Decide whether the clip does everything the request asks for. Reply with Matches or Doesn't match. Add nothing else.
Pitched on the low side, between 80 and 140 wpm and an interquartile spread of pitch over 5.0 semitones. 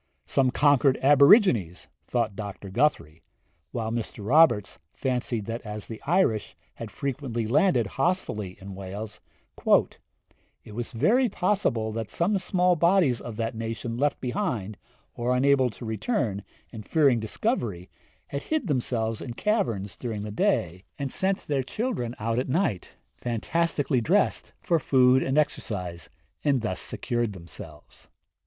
Matches